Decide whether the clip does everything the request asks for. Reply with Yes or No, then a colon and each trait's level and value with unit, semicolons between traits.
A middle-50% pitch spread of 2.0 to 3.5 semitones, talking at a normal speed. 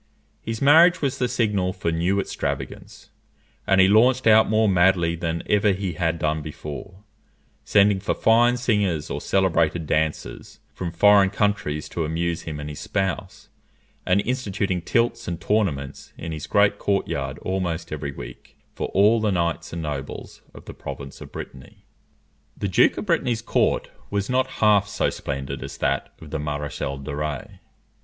No: average, 5.0 semitones; average, 165 wpm